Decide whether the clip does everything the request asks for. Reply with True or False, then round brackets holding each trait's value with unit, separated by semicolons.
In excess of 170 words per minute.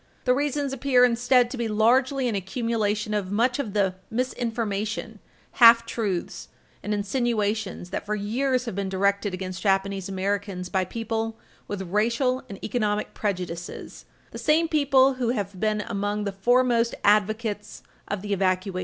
False (150 wpm)